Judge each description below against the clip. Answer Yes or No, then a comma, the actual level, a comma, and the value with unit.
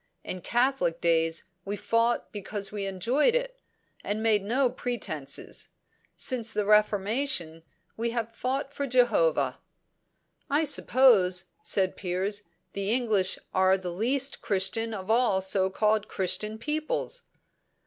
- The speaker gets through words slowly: Yes, slow, 125 wpm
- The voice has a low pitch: No, high, 215 Hz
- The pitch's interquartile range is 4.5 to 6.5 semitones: Yes, average, 4.8 semitones